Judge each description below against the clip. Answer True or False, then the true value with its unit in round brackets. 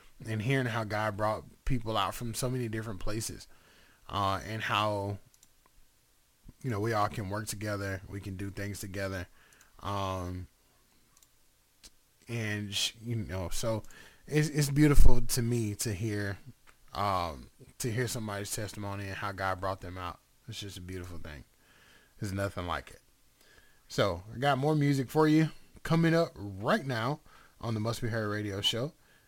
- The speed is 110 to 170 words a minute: True (160 wpm)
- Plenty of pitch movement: False (3.9 semitones)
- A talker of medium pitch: False (105 Hz)